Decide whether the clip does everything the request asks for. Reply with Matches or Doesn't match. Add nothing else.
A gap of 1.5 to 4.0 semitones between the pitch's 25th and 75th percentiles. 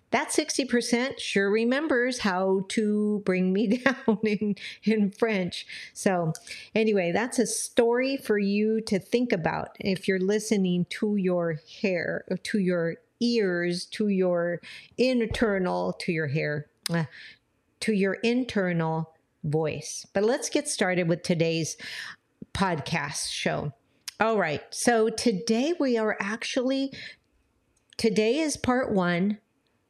Doesn't match